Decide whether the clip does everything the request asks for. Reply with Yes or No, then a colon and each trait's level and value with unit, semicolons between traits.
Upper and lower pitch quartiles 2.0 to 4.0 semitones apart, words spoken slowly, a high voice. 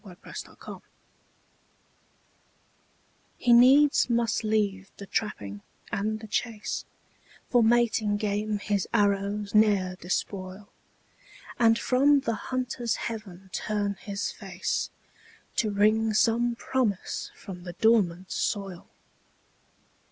Yes: average, 2.7 semitones; slow, 105 wpm; high, 210 Hz